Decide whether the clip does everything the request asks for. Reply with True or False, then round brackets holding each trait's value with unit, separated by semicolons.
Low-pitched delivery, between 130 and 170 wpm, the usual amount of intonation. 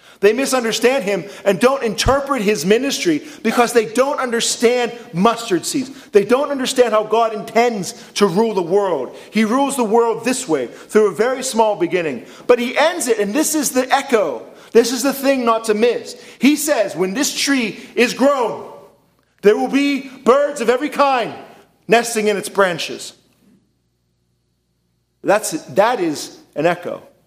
False (235 Hz; 165 wpm; 4.2 semitones)